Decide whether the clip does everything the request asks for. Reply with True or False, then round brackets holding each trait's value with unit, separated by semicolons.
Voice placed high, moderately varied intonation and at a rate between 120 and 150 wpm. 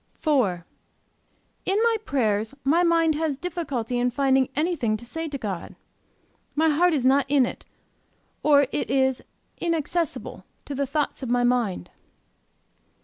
True (275 Hz; 4.6 semitones; 145 wpm)